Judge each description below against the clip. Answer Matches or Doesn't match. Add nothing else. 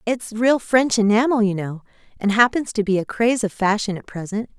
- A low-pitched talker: Doesn't match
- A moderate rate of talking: Doesn't match